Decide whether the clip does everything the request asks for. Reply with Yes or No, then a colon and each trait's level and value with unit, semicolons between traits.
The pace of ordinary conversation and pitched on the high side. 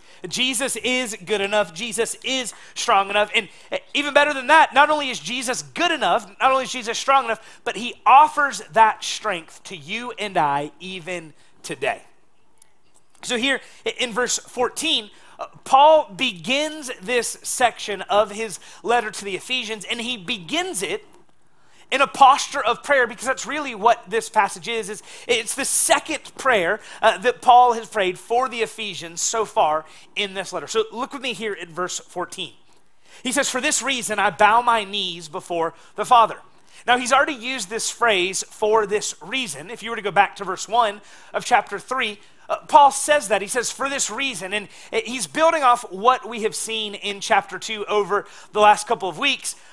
Yes: average, 185 wpm; high, 225 Hz